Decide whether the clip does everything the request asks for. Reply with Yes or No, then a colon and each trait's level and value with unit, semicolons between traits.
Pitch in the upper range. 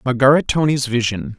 No: low, 130 Hz